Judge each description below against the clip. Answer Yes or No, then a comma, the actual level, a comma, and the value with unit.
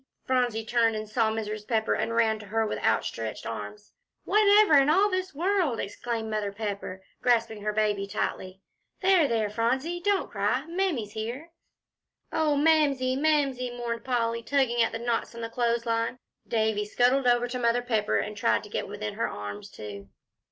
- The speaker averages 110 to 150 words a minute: No, average, 175 wpm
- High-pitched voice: Yes, high, 230 Hz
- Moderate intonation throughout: Yes, average, 4.0 semitones